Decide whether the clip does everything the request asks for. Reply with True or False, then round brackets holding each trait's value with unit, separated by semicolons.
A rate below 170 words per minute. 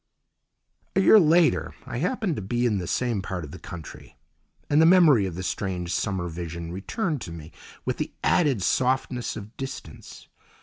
False (175 wpm)